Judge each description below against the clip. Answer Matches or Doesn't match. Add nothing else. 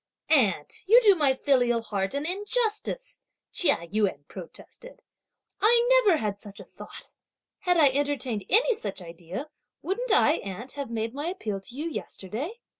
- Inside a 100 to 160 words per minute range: Matches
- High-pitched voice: Matches